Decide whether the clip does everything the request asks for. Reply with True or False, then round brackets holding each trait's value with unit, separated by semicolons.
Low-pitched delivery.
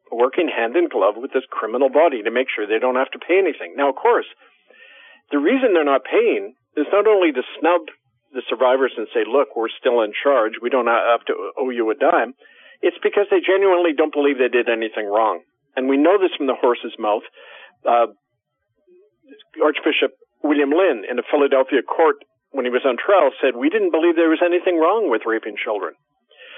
False (205 Hz)